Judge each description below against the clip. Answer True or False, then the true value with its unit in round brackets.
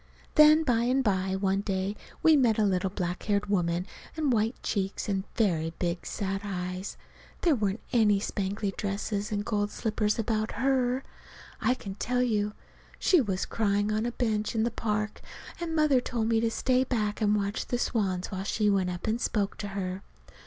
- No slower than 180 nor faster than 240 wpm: True (185 wpm)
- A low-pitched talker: False (210 Hz)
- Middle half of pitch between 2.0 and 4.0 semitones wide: True (3.2 semitones)